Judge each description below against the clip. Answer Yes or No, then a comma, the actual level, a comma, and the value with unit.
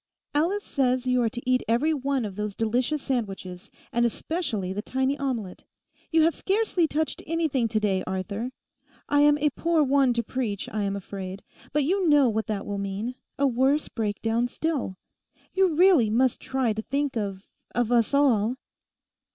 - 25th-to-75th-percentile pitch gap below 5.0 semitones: No, average, 5.3 semitones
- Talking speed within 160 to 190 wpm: Yes, average, 165 wpm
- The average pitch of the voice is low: No, very high, 250 Hz